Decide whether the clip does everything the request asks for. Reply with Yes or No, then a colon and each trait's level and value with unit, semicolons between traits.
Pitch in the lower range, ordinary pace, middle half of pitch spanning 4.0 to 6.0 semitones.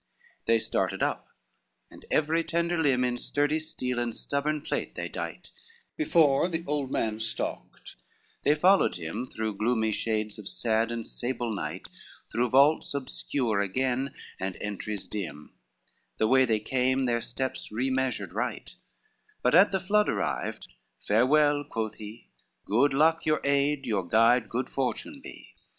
Yes: low, 125 Hz; average, 150 wpm; average, 4.7 semitones